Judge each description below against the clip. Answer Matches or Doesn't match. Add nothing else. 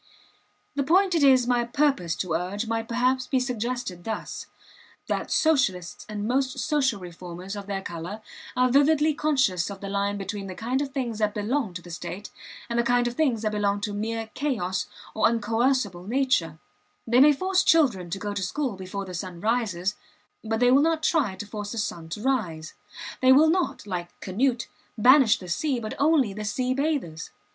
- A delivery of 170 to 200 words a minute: Matches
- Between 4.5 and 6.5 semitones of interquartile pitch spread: Matches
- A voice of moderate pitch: Doesn't match